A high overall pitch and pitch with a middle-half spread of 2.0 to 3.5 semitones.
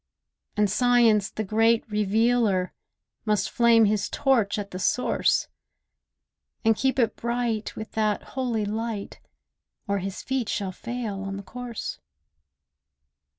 Yes: high, 220 Hz; narrow, 2.6 semitones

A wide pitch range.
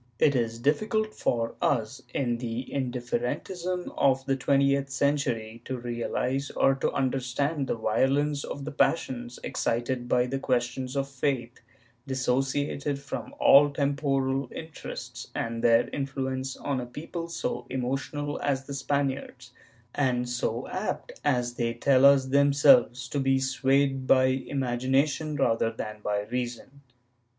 No: narrow, 2.4 semitones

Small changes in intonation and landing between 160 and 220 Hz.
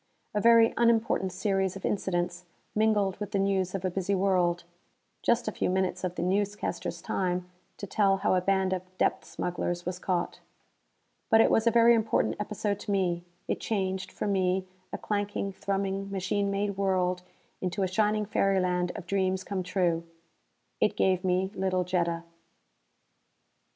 Yes: narrow, 1.9 semitones; high, 190 Hz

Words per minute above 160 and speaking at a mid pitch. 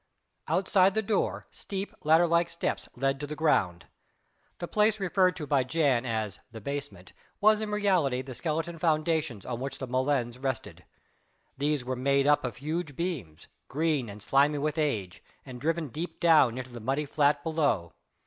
Yes: average, 170 wpm; medium, 145 Hz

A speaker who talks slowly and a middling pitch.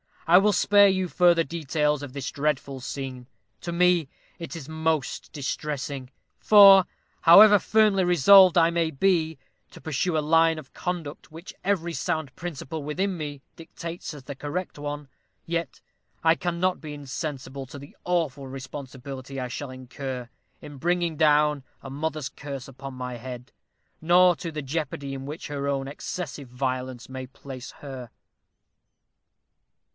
No: average, 150 wpm; medium, 150 Hz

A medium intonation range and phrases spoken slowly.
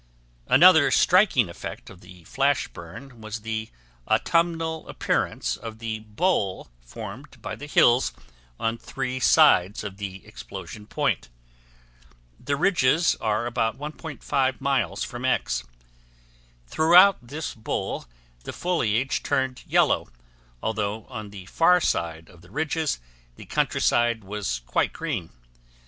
No: wide, 6.3 semitones; slow, 125 wpm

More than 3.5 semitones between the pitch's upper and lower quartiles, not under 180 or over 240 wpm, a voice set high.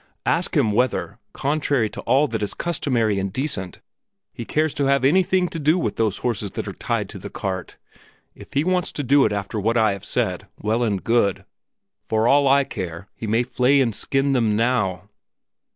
No: average, 5.1 semitones; average, 200 wpm; low, 120 Hz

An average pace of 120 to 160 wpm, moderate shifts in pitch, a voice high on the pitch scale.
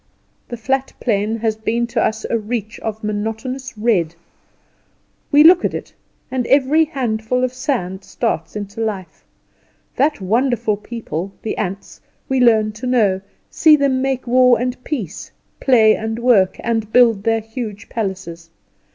Yes: average, 150 wpm; average, 3.3 semitones; high, 225 Hz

